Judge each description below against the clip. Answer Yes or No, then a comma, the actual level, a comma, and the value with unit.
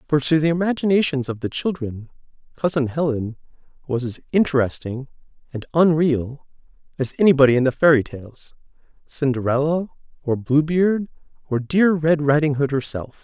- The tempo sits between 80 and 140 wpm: Yes, slow, 135 wpm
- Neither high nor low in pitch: Yes, medium, 145 Hz